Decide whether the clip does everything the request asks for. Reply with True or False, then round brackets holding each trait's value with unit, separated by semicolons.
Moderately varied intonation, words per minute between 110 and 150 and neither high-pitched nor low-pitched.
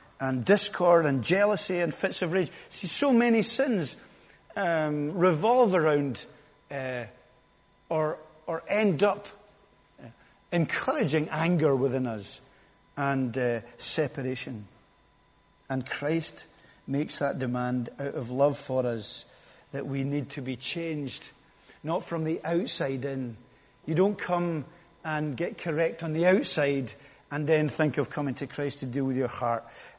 True (4.5 semitones; 140 wpm; 150 Hz)